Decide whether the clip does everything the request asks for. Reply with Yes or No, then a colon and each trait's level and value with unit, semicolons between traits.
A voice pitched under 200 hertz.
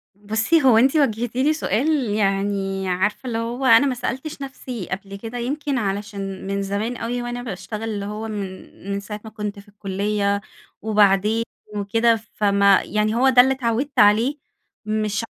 No: high, 215 Hz